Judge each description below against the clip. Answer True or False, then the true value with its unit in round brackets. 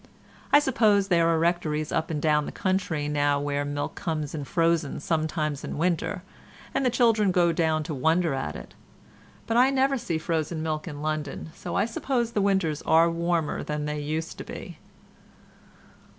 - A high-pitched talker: False (160 Hz)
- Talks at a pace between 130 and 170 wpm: False (185 wpm)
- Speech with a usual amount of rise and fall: True (3.5 semitones)